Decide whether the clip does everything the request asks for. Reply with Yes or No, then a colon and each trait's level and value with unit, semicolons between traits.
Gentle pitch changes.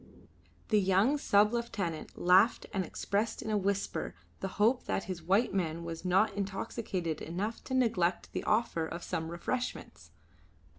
No: average, 4.1 semitones